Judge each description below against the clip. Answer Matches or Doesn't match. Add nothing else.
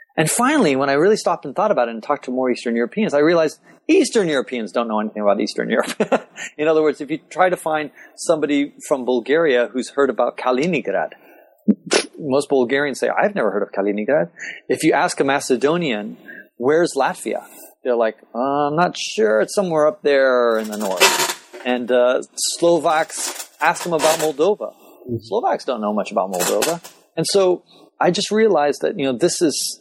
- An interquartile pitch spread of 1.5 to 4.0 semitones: Doesn't match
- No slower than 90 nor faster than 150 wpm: Doesn't match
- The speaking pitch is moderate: Matches